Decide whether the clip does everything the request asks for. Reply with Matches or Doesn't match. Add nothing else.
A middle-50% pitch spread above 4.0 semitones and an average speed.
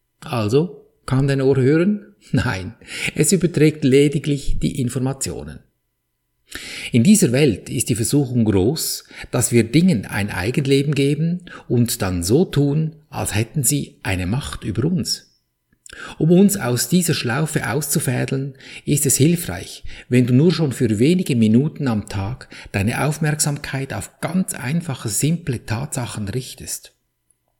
Matches